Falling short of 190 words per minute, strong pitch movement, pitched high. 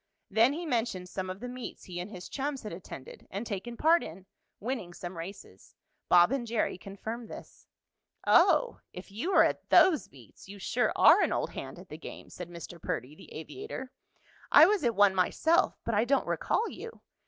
No: average, 195 wpm; wide, 6.4 semitones; high, 210 Hz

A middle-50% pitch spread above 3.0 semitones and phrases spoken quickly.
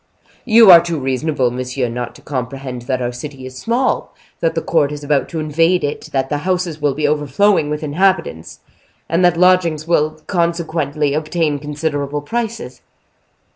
No: average, 3.7 semitones; average, 165 wpm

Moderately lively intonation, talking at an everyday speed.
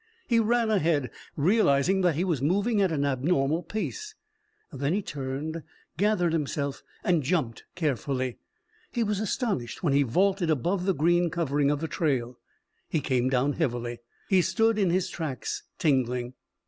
No: wide, 5.7 semitones; average, 155 wpm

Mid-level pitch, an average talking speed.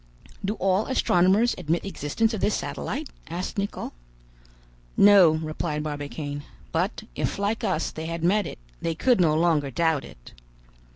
Yes: medium, 170 Hz; average, 155 wpm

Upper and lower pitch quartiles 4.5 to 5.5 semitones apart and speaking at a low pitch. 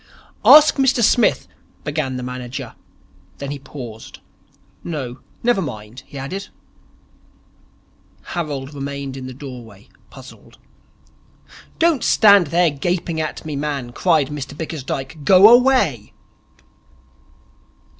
No: average, 5.1 semitones; medium, 145 Hz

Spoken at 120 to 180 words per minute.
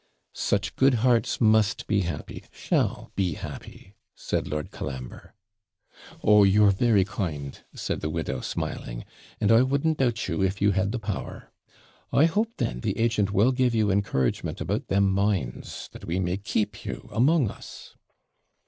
Yes: average, 155 wpm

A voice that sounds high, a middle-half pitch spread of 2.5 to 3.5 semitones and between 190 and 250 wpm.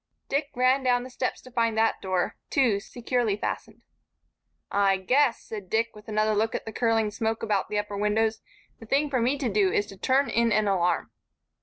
Yes: high, 225 Hz; average, 3.1 semitones; average, 200 wpm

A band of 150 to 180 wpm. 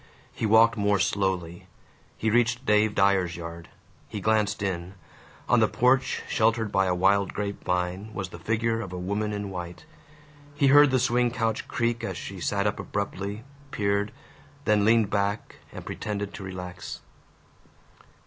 Yes: average, 160 wpm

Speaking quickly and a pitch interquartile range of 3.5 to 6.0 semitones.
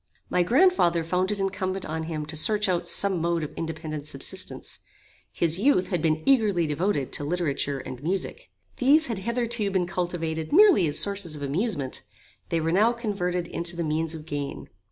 No: average, 180 wpm; average, 4.2 semitones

